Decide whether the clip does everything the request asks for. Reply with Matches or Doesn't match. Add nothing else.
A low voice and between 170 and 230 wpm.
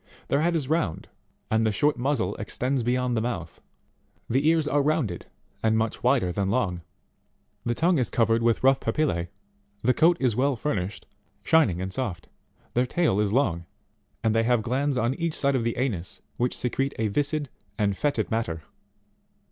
Matches